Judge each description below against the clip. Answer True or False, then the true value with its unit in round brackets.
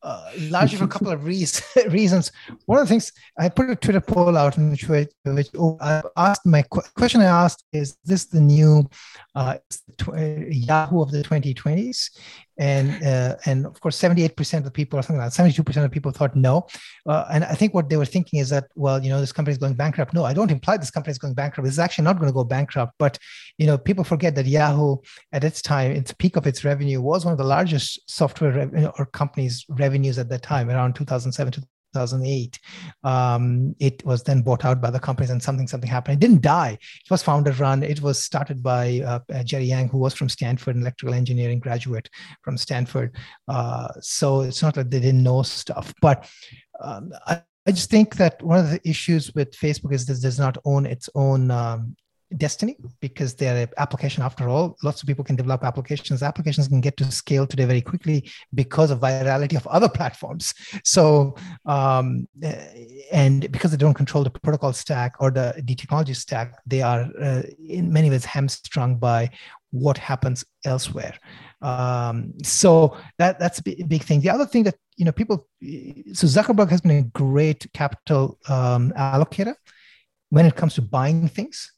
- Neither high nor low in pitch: True (145 Hz)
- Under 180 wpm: False (200 wpm)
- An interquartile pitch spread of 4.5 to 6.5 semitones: False (3.6 semitones)